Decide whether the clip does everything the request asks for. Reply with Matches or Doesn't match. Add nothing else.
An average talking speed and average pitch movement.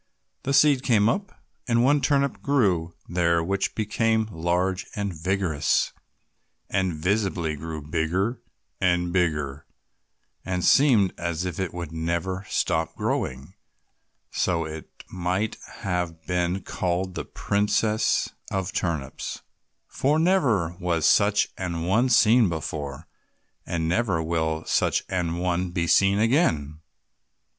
Doesn't match